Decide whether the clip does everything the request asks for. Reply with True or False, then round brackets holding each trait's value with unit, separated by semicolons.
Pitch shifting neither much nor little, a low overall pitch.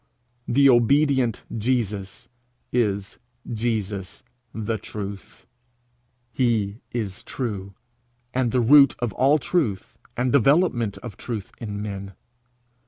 True (3.7 semitones; 115 Hz)